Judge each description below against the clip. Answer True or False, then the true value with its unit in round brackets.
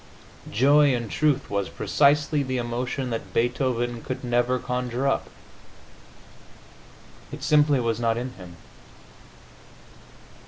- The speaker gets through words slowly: True (110 wpm)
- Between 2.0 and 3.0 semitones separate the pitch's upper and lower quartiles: True (2.7 semitones)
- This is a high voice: False (125 Hz)